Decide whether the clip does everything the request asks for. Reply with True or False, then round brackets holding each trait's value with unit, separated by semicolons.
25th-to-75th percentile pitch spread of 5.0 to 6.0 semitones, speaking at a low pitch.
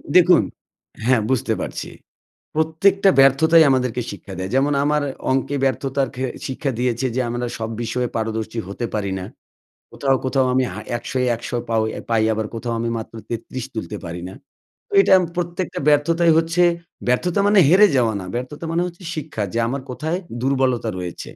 True (5.5 semitones; 130 Hz)